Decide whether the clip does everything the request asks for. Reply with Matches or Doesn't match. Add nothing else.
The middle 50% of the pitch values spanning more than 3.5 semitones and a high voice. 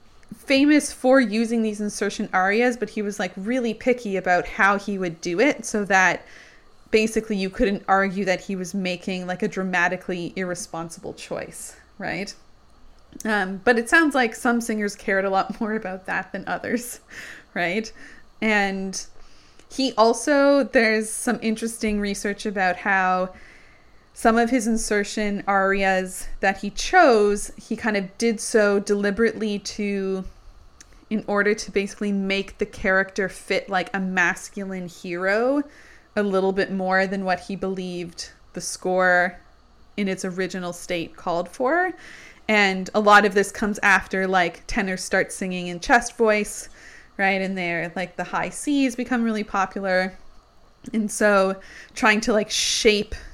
Doesn't match